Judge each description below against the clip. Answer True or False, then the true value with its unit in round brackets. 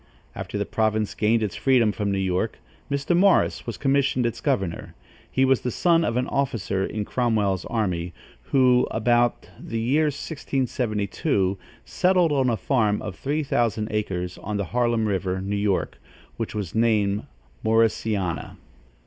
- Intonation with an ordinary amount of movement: True (4.4 semitones)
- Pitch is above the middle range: False (110 Hz)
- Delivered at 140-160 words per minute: True (150 wpm)